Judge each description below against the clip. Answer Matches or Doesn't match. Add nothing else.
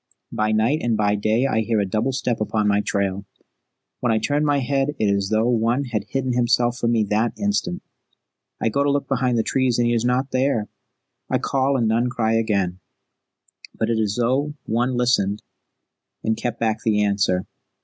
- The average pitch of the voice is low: Matches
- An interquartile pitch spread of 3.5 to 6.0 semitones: Doesn't match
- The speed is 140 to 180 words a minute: Doesn't match